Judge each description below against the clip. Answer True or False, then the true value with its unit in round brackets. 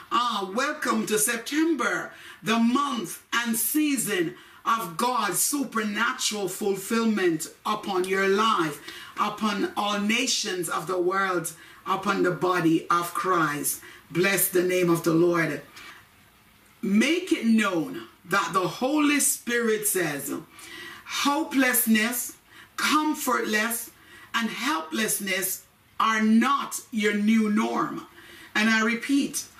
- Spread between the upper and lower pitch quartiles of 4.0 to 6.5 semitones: True (5.2 semitones)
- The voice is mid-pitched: False (215 Hz)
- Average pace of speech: False (105 wpm)